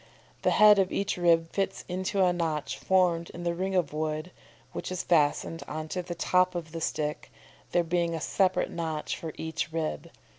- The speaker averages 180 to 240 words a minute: Yes, average, 190 wpm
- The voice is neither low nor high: Yes, medium, 170 Hz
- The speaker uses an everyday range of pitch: No, narrow, 2.3 semitones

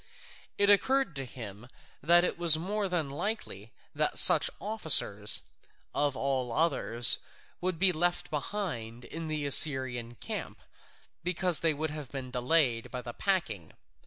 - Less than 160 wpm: Yes, slow, 135 wpm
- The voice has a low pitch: No, medium, 150 Hz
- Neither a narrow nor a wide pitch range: No, wide, 6.2 semitones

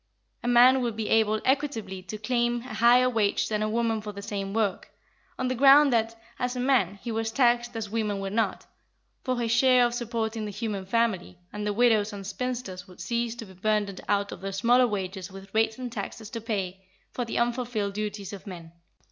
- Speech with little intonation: No, average, 3.0 semitones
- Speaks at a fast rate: Yes, fast, 210 wpm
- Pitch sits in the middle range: No, high, 220 Hz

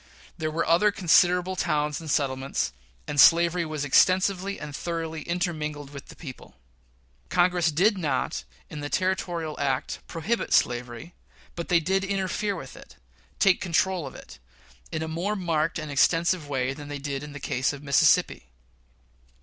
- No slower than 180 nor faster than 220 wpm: No, average, 160 wpm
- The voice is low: No, medium, 160 Hz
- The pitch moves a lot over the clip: No, average, 3.7 semitones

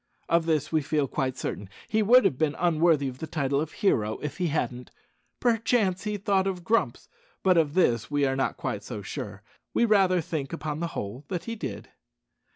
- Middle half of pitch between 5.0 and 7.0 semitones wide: Yes, wide, 5.6 semitones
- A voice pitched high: No, medium, 160 Hz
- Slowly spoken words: No, average, 195 wpm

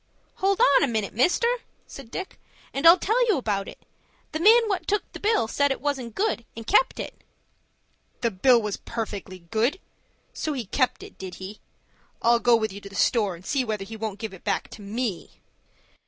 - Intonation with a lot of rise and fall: Yes, wide, 6.3 semitones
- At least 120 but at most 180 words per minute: No, fast, 205 wpm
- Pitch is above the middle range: Yes, high, 235 Hz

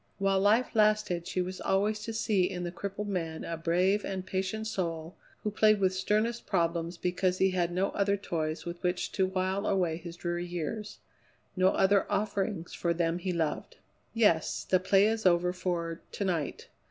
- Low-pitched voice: No, medium, 185 Hz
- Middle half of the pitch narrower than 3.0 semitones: Yes, narrow, 2.6 semitones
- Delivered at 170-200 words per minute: Yes, average, 180 wpm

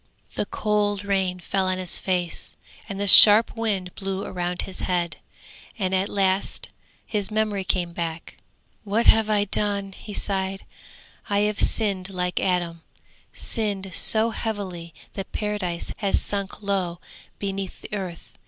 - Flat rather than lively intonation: Yes, narrow, 2.0 semitones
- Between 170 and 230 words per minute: No, average, 145 wpm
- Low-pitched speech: No, high, 195 Hz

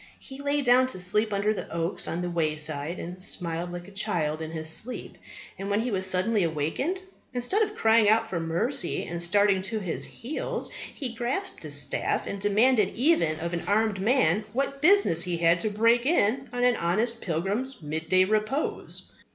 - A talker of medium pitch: No, high, 205 Hz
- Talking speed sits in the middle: Yes, average, 185 wpm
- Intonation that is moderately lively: No, wide, 6.2 semitones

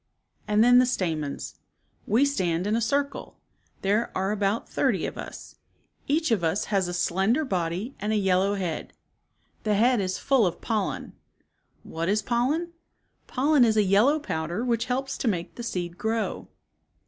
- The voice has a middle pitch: No, high, 215 Hz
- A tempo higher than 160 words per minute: Yes, average, 170 wpm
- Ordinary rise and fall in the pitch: Yes, average, 4.9 semitones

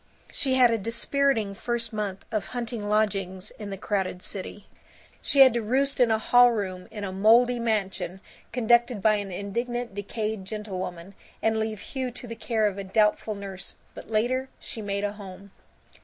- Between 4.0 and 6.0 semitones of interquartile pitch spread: No, average, 3.1 semitones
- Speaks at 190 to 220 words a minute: No, average, 175 wpm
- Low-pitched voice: No, high, 215 Hz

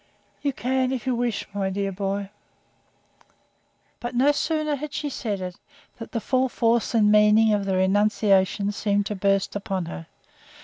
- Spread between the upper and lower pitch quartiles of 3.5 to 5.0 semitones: Yes, average, 4.1 semitones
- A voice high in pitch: Yes, high, 210 Hz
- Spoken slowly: No, average, 165 wpm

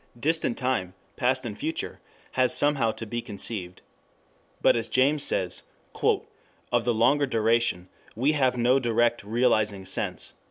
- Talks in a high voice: No, low, 120 Hz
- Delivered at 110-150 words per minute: Yes, slow, 135 wpm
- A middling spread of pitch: Yes, average, 3.1 semitones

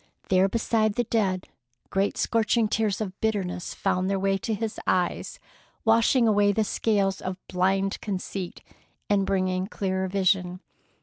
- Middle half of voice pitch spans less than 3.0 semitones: Yes, narrow, 2.5 semitones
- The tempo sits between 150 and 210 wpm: No, average, 140 wpm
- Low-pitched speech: No, high, 195 Hz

